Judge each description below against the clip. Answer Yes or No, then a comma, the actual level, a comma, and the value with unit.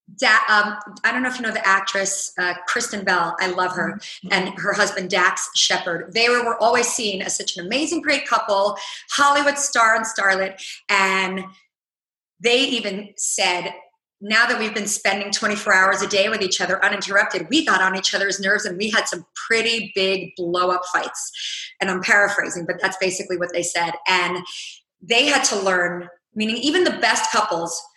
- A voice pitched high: Yes, high, 200 Hz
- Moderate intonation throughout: Yes, average, 3.3 semitones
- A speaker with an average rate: Yes, average, 185 wpm